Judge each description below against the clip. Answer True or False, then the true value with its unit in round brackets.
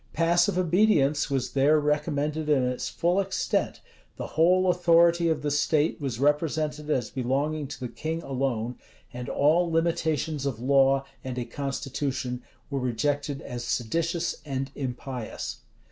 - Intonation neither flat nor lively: True (3.4 semitones)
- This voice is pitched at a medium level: True (145 Hz)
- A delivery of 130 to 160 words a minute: True (140 wpm)